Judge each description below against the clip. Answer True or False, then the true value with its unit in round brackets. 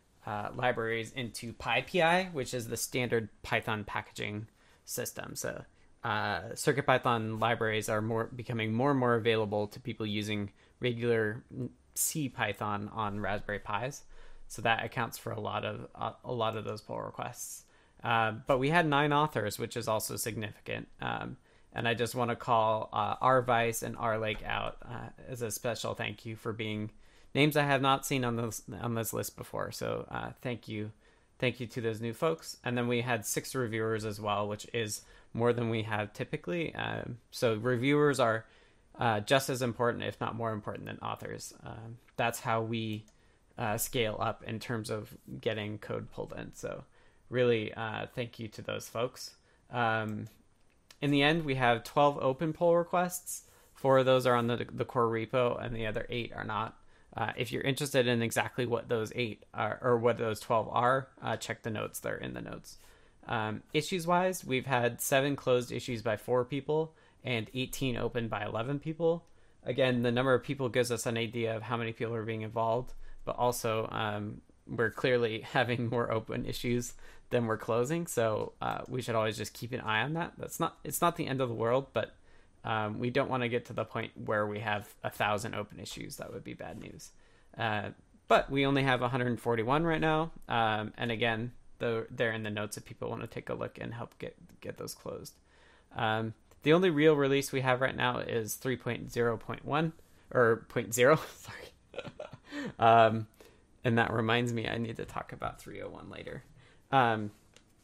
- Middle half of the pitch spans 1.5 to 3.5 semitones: True (2.7 semitones)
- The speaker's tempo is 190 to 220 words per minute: True (195 wpm)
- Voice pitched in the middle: False (115 Hz)